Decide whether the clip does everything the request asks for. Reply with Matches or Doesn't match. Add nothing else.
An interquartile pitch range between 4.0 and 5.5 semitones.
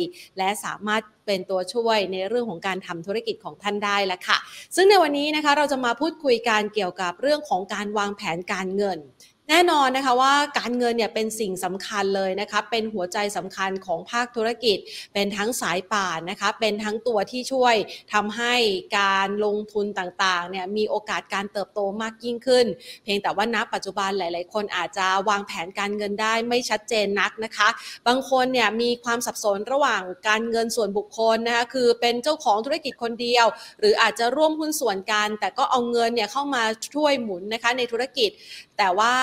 Doesn't match